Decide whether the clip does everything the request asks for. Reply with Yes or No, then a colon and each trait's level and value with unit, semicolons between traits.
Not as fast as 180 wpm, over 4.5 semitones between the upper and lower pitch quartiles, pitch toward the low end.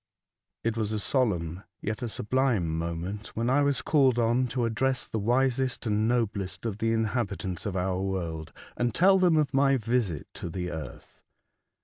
Yes: average, 170 wpm; average, 5.1 semitones; low, 115 Hz